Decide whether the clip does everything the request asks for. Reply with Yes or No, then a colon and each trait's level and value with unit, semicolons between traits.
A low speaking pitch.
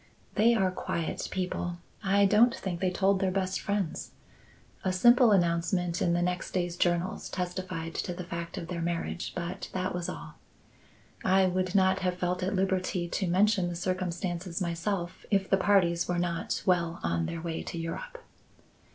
No: medium, 180 Hz